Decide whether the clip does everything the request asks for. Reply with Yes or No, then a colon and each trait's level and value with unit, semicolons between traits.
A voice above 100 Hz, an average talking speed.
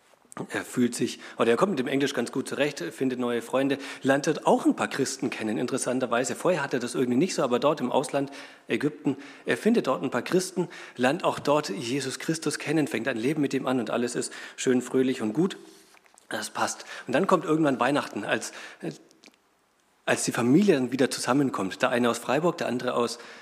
No: low, 135 Hz; fast, 205 wpm